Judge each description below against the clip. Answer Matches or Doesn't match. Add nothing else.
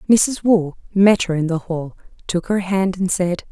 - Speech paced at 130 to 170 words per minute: Doesn't match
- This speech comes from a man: Doesn't match